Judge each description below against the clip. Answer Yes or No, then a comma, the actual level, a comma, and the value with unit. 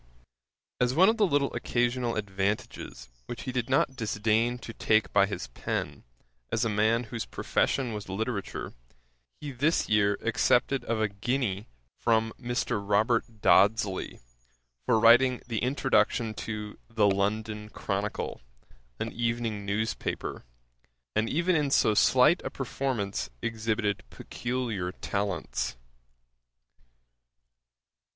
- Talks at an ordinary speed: No, slow, 120 wpm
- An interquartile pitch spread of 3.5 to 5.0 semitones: No, average, 3.0 semitones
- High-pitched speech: No, low, 115 Hz